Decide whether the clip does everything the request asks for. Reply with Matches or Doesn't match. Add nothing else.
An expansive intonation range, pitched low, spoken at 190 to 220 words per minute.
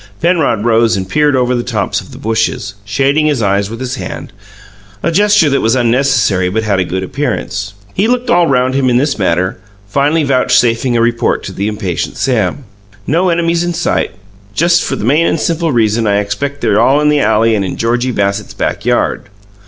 Matches